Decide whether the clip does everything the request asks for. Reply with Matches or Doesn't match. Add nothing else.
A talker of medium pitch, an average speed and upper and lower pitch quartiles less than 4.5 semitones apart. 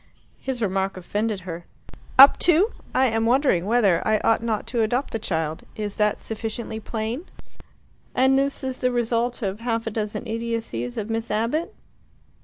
Doesn't match